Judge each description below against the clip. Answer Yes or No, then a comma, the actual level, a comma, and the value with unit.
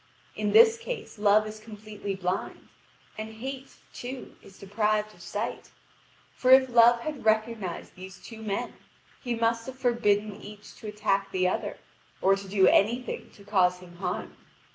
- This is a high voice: Yes, high, 215 Hz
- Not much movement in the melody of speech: No, average, 3.1 semitones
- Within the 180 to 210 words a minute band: No, average, 165 wpm